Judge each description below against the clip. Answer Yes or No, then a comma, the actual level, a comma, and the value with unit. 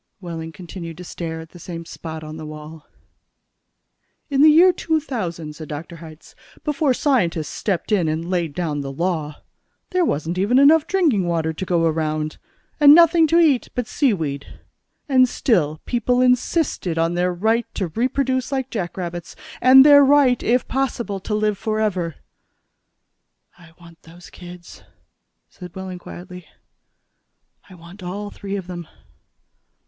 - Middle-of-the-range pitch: Yes, medium, 180 Hz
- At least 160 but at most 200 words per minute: No, average, 150 wpm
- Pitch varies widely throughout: Yes, wide, 7.3 semitones